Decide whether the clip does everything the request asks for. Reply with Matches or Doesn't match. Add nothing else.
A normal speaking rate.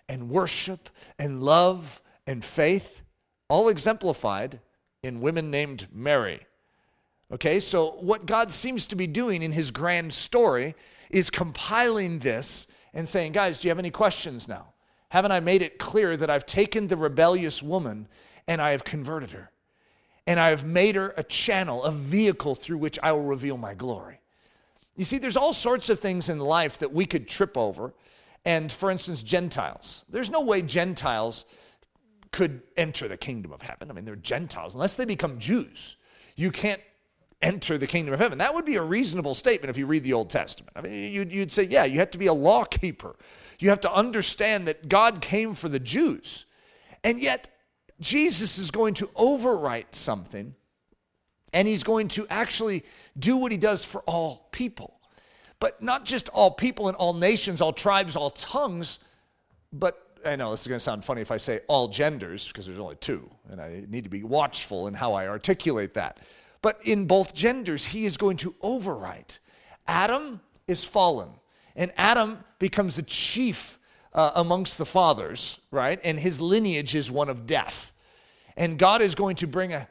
Matches